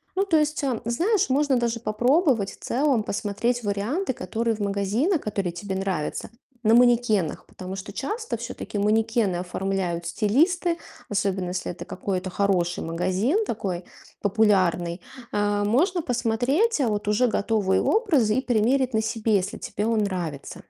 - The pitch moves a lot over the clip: No, average, 4.7 semitones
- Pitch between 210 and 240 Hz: Yes, high, 215 Hz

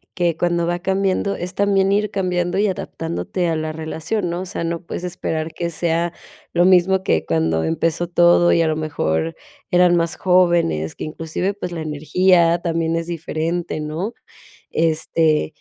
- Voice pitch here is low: No, medium, 170 Hz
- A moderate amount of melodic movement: No, narrow, 2.3 semitones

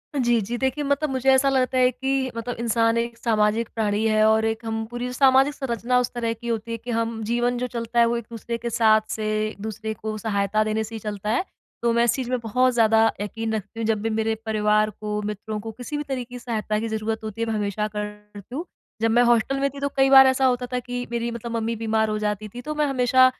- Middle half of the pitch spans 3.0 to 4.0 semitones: No, narrow, 2.4 semitones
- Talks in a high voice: Yes, high, 230 Hz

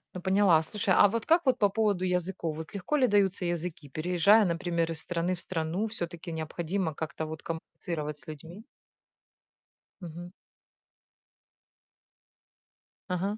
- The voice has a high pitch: No, medium, 175 Hz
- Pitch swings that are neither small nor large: Yes, average, 3.5 semitones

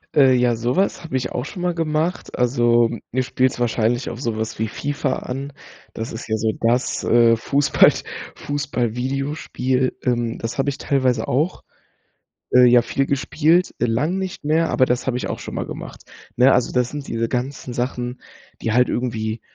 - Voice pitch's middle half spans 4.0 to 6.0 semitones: No, average, 2.9 semitones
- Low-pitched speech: Yes, low, 125 Hz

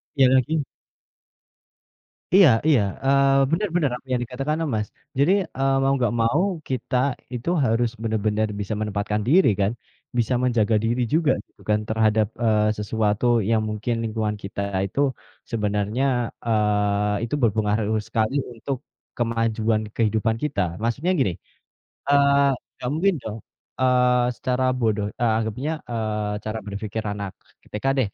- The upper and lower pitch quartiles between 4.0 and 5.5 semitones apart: No, average, 3.6 semitones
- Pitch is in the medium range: No, low, 115 Hz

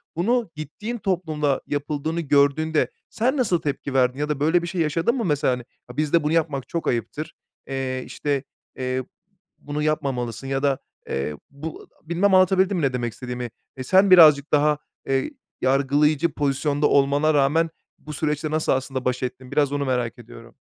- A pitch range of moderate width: Yes, average, 3.3 semitones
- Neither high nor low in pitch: Yes, medium, 145 Hz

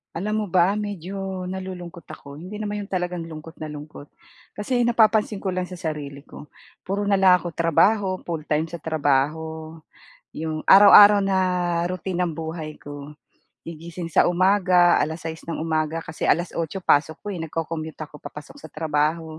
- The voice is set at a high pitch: No, medium, 170 Hz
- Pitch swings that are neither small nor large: Yes, average, 3.3 semitones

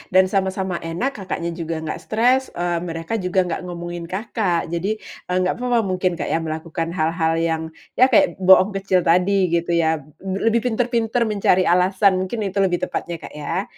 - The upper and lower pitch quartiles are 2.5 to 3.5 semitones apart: Yes, average, 3.2 semitones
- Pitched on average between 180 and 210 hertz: Yes, medium, 185 Hz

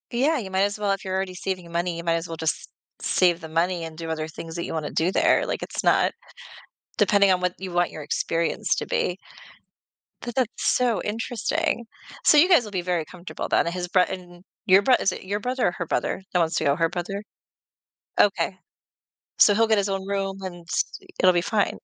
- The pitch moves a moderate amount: Yes, average, 3.1 semitones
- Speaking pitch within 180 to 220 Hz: Yes, medium, 185 Hz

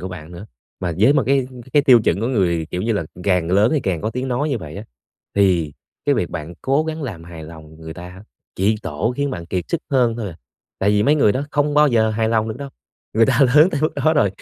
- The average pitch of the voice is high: No, low, 110 Hz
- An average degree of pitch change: No, wide, 7.3 semitones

